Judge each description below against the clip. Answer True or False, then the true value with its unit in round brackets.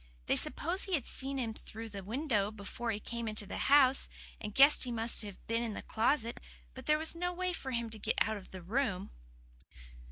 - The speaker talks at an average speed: False (215 wpm)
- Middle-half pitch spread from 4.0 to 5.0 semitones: True (4.4 semitones)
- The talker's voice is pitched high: True (230 Hz)